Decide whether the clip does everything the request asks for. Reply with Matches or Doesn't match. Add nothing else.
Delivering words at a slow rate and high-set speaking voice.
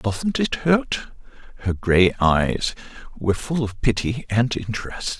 Doesn't match